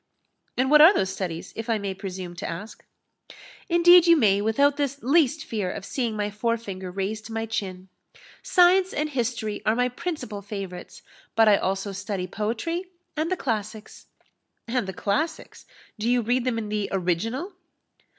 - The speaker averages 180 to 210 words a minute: No, average, 170 wpm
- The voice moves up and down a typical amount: No, wide, 5.9 semitones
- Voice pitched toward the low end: No, high, 225 Hz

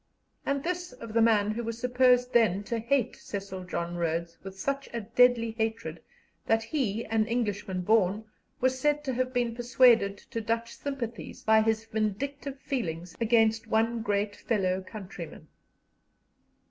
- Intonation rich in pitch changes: No, average, 3.4 semitones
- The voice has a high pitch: Yes, high, 225 Hz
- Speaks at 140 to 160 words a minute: Yes, average, 150 wpm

